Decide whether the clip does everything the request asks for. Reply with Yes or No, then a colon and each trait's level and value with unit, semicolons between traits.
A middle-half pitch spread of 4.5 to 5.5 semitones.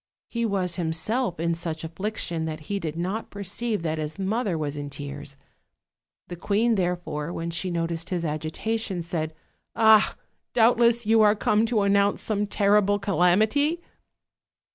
Yes: average, 4.8 semitones